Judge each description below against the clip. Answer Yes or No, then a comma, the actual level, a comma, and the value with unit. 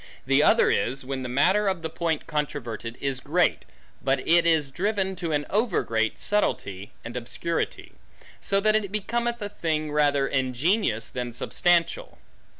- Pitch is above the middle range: No, medium, 155 Hz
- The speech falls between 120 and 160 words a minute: Yes, average, 155 wpm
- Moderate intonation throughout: No, wide, 6.6 semitones